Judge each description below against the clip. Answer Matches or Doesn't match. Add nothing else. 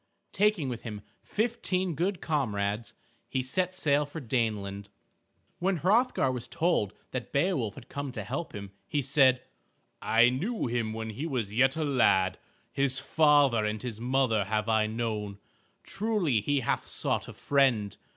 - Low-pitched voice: Matches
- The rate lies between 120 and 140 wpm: Doesn't match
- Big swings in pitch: Matches